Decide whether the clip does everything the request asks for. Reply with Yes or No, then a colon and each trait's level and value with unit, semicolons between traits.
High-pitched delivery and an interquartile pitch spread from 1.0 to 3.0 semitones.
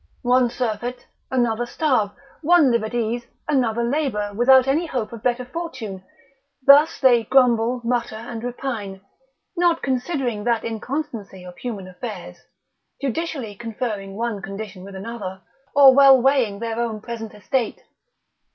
No: high, 235 Hz; average, 3.5 semitones